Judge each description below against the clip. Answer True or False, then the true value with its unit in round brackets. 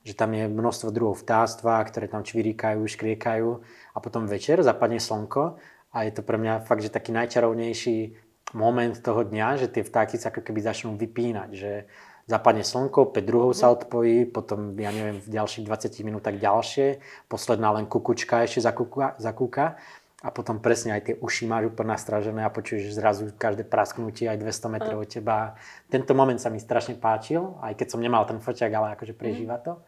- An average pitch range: False (1.5 semitones)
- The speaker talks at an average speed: False (185 wpm)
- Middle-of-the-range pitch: False (115 Hz)